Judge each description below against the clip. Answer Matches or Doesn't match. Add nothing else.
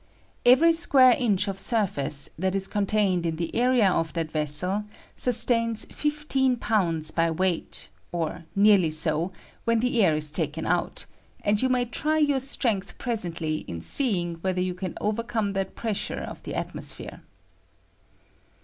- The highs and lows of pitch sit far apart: Matches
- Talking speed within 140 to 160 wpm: Matches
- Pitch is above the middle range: Matches